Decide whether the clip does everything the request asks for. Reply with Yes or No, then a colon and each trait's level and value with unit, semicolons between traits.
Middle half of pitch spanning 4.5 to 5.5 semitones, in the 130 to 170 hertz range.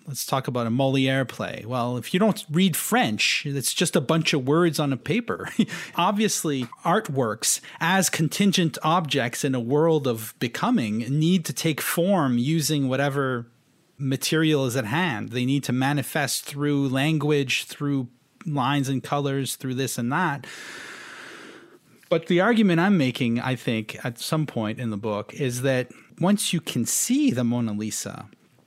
Yes: average, 4.8 semitones; medium, 140 Hz